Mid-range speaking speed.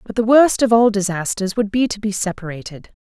No: fast, 215 wpm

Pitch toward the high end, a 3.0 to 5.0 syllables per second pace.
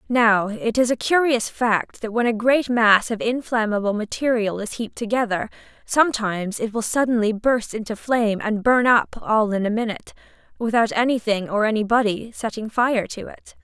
No: high, 225 Hz; 5.2 syllables/s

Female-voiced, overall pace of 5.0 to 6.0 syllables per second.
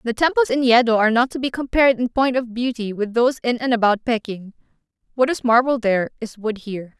No: female; 6.2 syllables/s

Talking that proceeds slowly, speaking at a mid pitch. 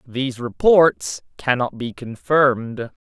No: slow, 100 wpm; low, 125 Hz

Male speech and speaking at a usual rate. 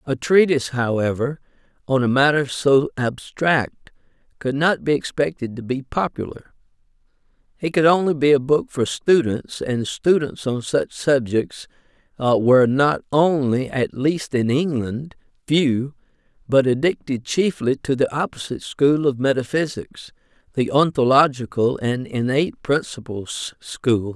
No: male; slow, 125 wpm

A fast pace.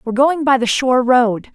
Yes: fast, 235 wpm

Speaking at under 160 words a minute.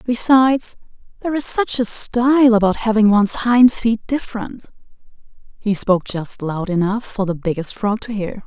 No: average, 165 wpm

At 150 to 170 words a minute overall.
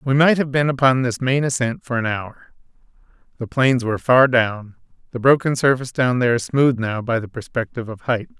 No: average, 200 wpm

